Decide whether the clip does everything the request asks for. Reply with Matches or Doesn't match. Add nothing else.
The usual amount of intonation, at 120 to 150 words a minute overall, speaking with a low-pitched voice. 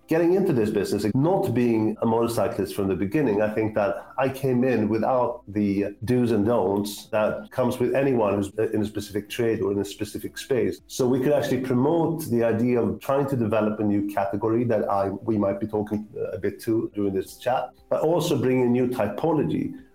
Doesn't match